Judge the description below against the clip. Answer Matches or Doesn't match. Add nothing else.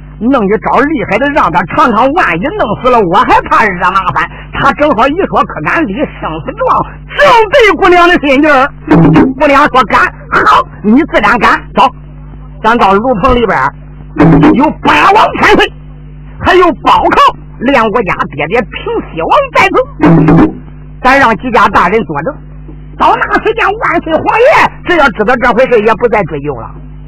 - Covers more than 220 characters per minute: Matches